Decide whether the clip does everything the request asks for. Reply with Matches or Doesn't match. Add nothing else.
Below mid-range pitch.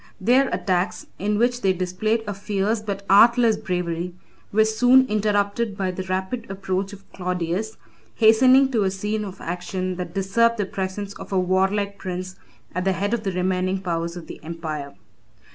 Doesn't match